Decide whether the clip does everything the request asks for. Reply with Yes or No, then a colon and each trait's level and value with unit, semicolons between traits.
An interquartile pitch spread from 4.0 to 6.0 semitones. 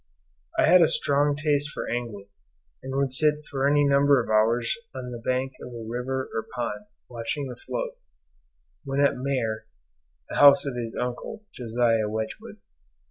No: average, 3.4 semitones